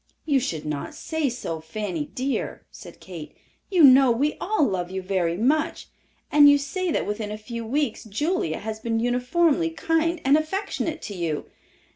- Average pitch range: No, wide, 7.8 semitones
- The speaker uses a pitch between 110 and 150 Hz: No, very high, 250 Hz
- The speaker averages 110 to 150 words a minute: No, average, 170 wpm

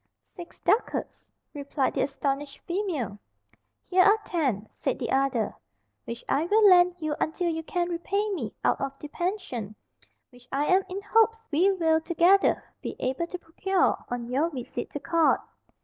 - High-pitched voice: Yes, very high, 325 Hz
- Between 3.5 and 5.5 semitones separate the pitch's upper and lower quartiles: Yes, average, 5.2 semitones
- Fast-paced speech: No, average, 165 wpm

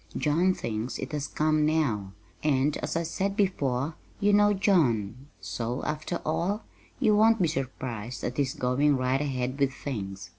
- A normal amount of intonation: Yes, average, 5.0 semitones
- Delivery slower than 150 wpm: No, average, 160 wpm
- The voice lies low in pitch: No, medium, 145 Hz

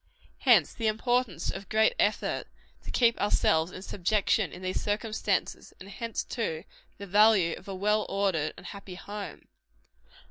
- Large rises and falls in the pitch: No, average, 2.8 semitones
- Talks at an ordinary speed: Yes, average, 150 wpm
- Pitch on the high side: Yes, high, 200 Hz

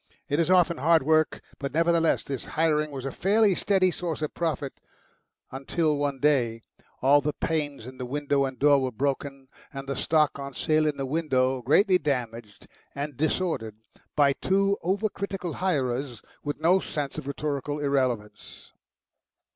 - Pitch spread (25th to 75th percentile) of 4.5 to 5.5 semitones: No, average, 3.4 semitones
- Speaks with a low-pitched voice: No, medium, 145 Hz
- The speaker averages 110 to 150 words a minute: No, average, 160 wpm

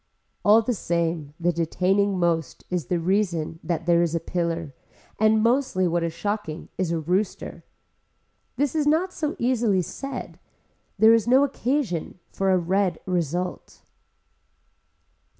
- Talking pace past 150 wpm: No, average, 140 wpm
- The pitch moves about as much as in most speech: Yes, average, 4.6 semitones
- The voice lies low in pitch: No, medium, 185 Hz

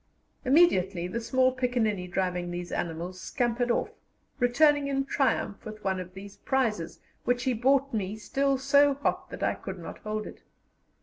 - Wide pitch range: Yes, wide, 5.9 semitones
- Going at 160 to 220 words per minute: Yes, average, 165 wpm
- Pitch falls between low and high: No, high, 235 Hz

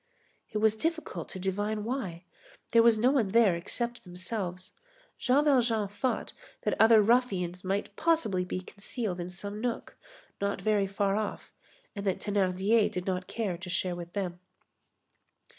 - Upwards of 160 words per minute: No, average, 155 wpm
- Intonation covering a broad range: No, average, 3.8 semitones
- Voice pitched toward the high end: Yes, high, 205 Hz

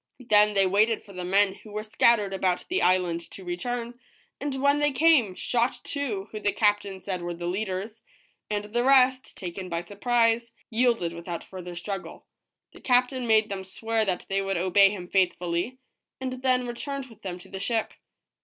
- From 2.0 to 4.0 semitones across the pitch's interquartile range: No, average, 4.4 semitones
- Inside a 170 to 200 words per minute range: Yes, average, 185 wpm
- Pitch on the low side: No, high, 210 Hz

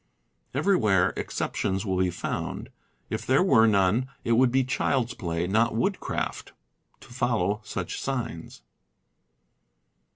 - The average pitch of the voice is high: No, low, 115 Hz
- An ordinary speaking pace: No, slow, 120 wpm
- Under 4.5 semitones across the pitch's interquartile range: No, average, 5.2 semitones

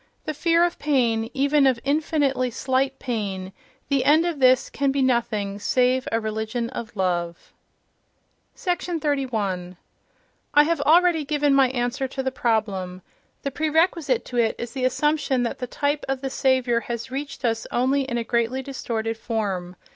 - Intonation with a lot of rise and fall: No, average, 3.8 semitones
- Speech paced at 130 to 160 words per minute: Yes, average, 155 wpm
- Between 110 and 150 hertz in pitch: No, very high, 255 Hz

